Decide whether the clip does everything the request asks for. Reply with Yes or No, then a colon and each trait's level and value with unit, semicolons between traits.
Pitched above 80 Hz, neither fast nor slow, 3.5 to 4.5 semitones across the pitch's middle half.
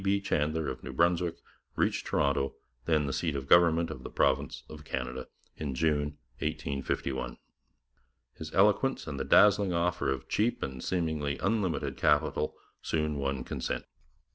No: very low, 75 Hz; average, 145 wpm; average, 3.8 semitones